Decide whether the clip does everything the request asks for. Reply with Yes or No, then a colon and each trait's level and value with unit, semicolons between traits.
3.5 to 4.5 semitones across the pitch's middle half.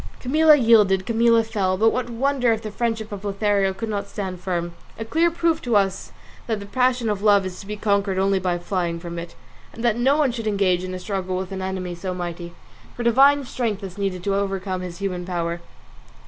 Yes: average, 3.8 semitones